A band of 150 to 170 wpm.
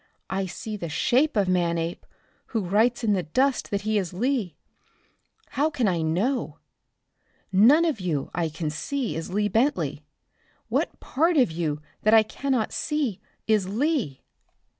Yes: average, 155 wpm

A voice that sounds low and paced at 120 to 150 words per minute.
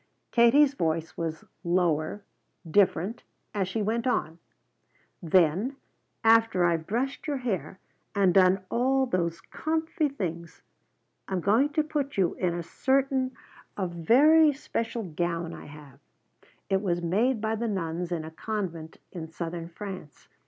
No: high, 190 Hz; average, 140 wpm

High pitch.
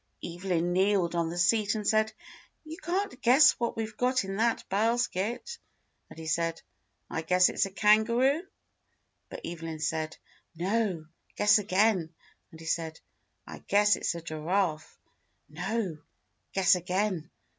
Yes: high, 195 Hz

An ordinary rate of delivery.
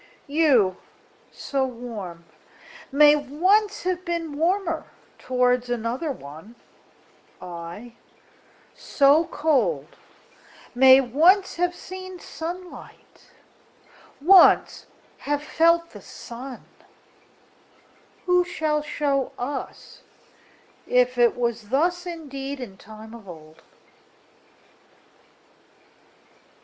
No: slow, 70 wpm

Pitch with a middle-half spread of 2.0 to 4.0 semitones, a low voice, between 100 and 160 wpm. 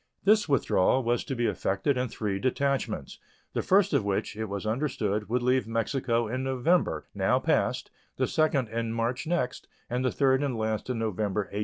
No: average, 3.5 semitones; low, 120 Hz; average, 185 wpm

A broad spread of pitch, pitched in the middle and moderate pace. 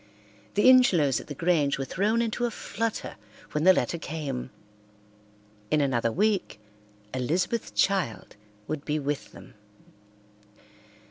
No: wide, 6.7 semitones; medium, 160 Hz; slow, 125 wpm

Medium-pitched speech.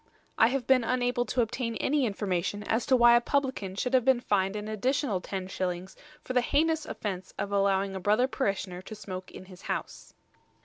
No: high, 215 Hz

